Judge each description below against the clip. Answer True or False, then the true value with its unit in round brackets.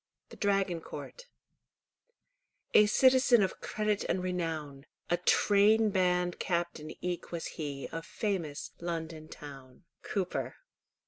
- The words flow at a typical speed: False (110 wpm)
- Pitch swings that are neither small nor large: True (4.1 semitones)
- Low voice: False (180 Hz)